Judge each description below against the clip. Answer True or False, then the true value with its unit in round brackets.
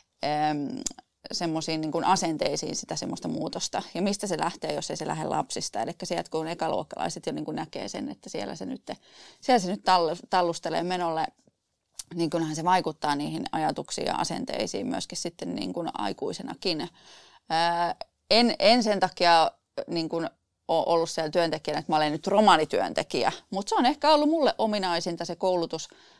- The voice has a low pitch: False (170 Hz)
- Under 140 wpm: False (145 wpm)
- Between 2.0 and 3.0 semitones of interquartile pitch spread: False (3.8 semitones)